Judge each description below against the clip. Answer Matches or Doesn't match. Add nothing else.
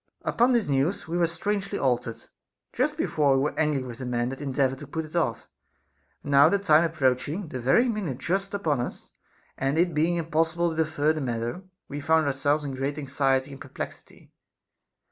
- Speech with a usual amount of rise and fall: Matches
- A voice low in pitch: Doesn't match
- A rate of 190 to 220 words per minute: Matches